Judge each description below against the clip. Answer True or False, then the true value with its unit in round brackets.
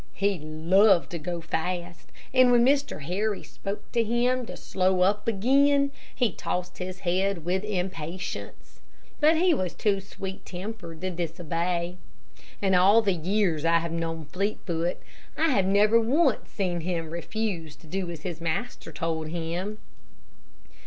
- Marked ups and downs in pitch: False (4.0 semitones)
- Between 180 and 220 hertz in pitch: True (185 Hz)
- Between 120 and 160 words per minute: True (150 wpm)